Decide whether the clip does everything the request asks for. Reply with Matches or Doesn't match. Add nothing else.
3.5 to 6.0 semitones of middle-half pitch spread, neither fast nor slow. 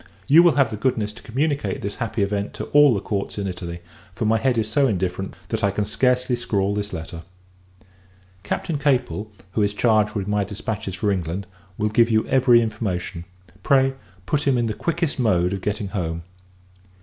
Matches